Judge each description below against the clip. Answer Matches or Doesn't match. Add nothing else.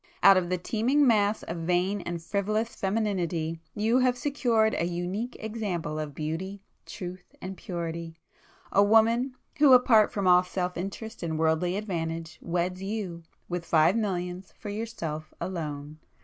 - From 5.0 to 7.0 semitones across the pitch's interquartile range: Doesn't match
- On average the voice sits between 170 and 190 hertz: Matches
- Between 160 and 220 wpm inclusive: Doesn't match